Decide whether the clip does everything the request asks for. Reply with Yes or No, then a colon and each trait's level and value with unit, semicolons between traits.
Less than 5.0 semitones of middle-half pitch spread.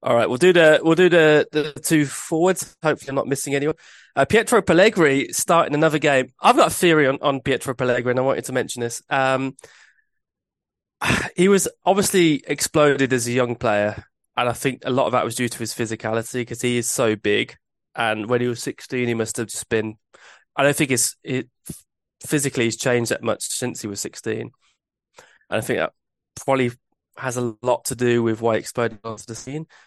Yes: average, 3.8 semitones